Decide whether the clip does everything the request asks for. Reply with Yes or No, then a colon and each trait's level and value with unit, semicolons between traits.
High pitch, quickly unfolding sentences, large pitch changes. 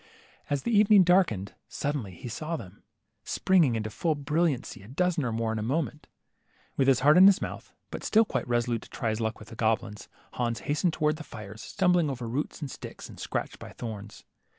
No: low, 135 Hz; fast, 210 wpm; wide, 6.6 semitones